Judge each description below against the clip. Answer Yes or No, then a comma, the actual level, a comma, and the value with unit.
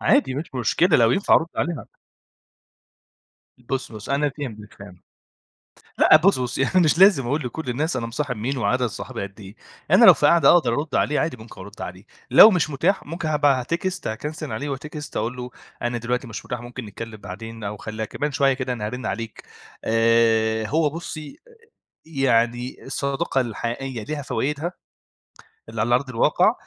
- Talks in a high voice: No, low, 125 Hz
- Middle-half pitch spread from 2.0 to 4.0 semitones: No, average, 4.7 semitones